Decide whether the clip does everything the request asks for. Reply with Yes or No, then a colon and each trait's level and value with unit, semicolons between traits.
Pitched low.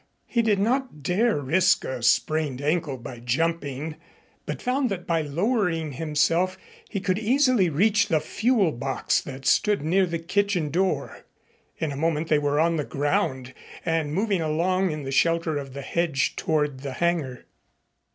No: medium, 165 Hz